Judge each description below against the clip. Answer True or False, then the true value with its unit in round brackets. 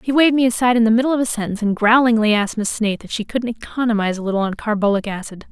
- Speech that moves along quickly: True (260 wpm)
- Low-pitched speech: False (225 Hz)